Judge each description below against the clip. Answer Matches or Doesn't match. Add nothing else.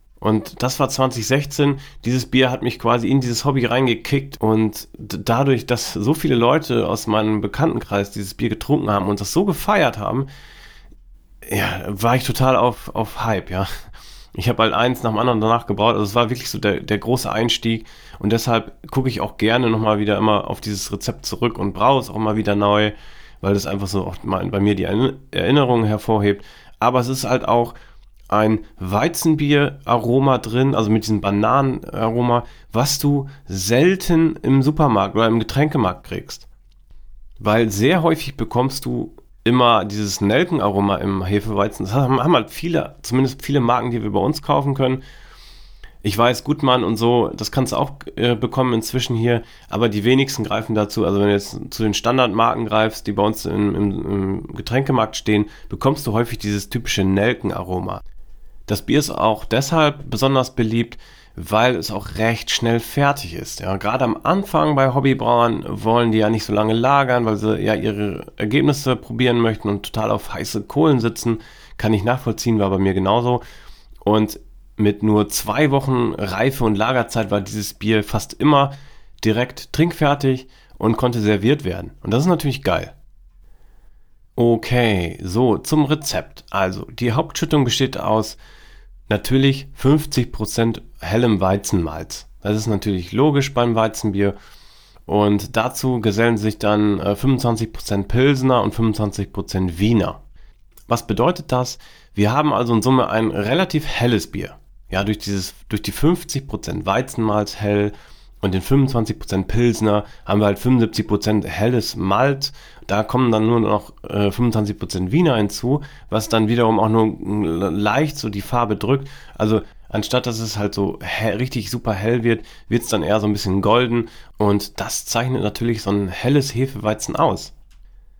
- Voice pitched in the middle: Doesn't match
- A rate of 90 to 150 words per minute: Doesn't match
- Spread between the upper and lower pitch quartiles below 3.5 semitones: Doesn't match